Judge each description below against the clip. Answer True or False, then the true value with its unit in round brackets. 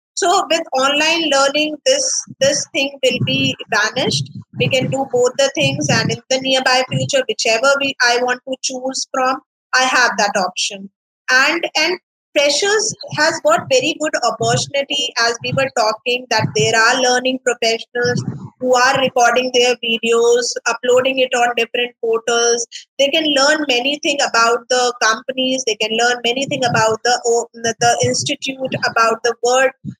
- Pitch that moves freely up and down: False (3.0 semitones)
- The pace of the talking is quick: False (160 wpm)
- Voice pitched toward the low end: False (255 Hz)